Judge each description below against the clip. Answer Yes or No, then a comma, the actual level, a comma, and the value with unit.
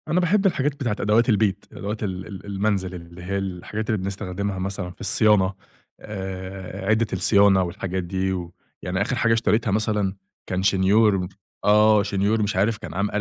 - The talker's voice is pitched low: Yes, low, 100 Hz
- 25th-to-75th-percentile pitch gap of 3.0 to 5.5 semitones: No, narrow, 2.4 semitones